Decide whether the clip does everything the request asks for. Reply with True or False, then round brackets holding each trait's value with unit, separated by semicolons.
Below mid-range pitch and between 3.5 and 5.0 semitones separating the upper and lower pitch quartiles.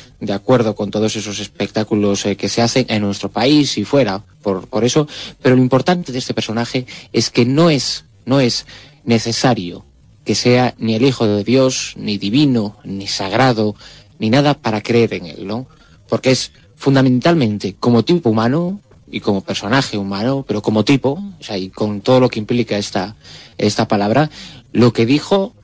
True (115 Hz; 4.0 semitones)